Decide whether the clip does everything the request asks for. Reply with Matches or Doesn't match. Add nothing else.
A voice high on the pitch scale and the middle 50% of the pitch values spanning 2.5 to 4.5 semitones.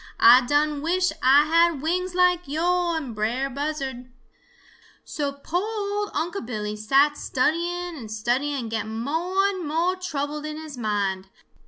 Doesn't match